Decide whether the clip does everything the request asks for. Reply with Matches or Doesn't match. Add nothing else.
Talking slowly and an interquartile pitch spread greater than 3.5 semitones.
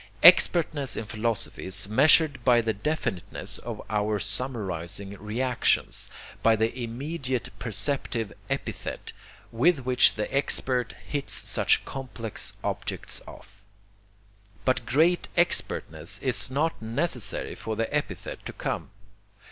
Matches